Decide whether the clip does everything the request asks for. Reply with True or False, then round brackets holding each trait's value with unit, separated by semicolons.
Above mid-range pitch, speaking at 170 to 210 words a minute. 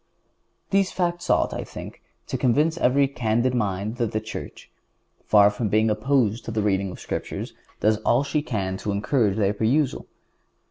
False (110 Hz; 175 wpm)